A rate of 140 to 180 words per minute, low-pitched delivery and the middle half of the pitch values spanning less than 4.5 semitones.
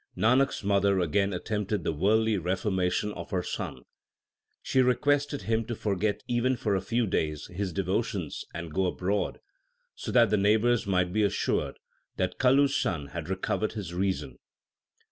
Yes: average, 165 wpm; low, 100 Hz; average, 3.9 semitones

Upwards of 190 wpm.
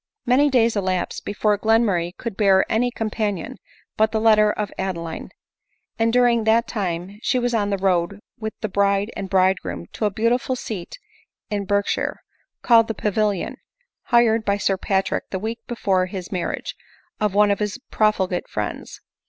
No: average, 160 wpm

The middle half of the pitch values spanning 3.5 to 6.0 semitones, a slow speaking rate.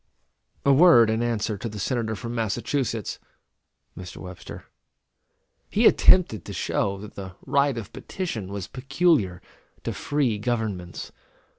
Yes: average, 4.9 semitones; slow, 130 wpm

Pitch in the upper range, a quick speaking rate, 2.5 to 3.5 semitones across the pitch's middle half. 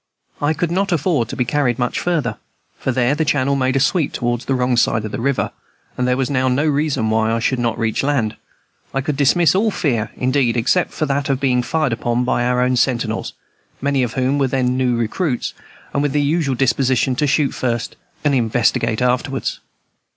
No: low, 130 Hz; fast, 210 wpm; average, 2.9 semitones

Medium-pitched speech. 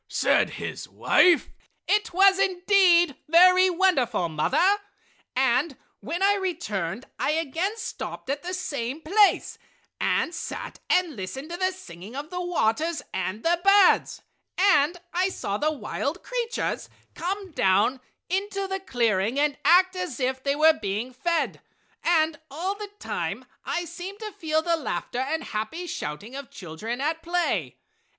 No: very high, 325 Hz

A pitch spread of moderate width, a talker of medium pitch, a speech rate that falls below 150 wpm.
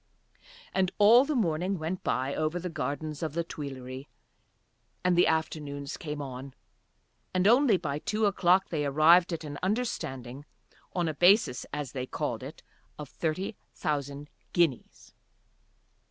Yes: average, 4.4 semitones; medium, 155 Hz; average, 140 wpm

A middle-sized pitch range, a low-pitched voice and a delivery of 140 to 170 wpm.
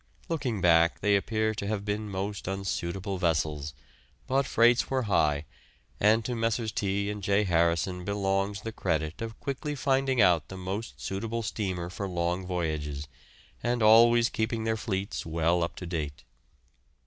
Yes: average, 4.5 semitones; low, 100 Hz; average, 155 wpm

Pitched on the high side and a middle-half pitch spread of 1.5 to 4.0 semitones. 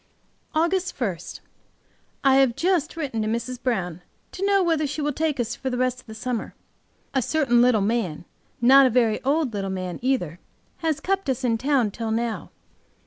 No: very high, 255 Hz; average, 4.8 semitones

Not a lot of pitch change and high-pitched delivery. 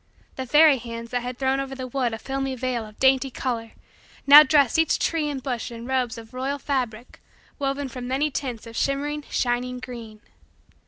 Yes: narrow, 2.3 semitones; very high, 260 Hz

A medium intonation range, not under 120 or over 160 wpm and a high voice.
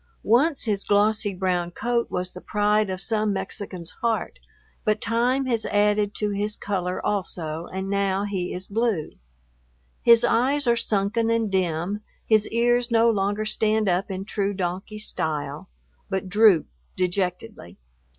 Yes: average, 3.1 semitones; average, 145 wpm; high, 205 Hz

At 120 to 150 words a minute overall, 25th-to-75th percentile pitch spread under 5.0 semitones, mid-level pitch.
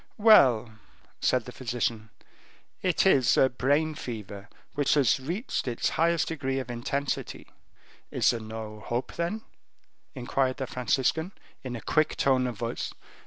No: average, 140 wpm; average, 4.1 semitones; low, 130 Hz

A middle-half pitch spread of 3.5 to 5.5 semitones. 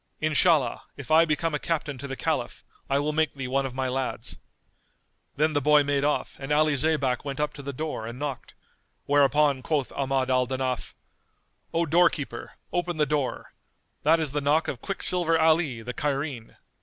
No: average, 2.7 semitones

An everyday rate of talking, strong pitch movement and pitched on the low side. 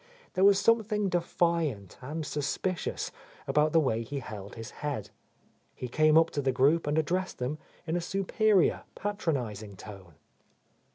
No: average, 150 wpm; wide, 6.1 semitones; medium, 155 Hz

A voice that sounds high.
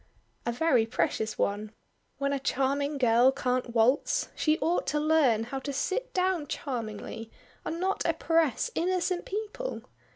Yes: very high, 280 Hz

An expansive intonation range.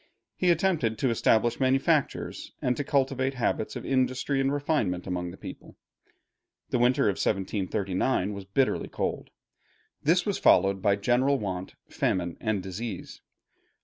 Yes: wide, 5.7 semitones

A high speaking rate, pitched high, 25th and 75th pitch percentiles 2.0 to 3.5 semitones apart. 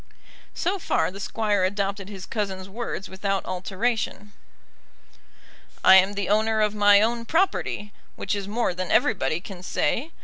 No: average, 145 wpm; high, 205 Hz; narrow, 2.5 semitones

